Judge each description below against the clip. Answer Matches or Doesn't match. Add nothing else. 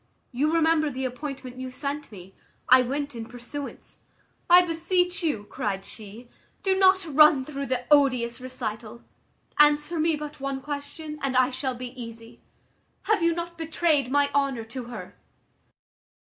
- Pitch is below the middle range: Doesn't match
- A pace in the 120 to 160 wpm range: Matches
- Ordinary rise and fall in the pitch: Matches